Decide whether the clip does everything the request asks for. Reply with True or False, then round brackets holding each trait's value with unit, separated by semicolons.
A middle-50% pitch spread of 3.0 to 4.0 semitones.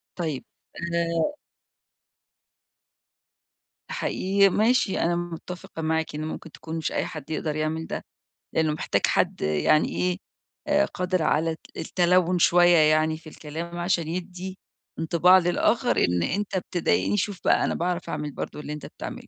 False (2.5 semitones)